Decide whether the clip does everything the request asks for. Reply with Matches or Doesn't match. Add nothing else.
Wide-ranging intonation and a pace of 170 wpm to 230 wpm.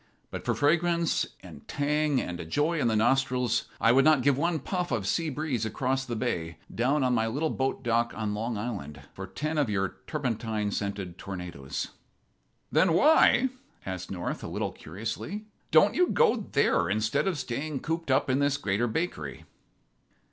Matches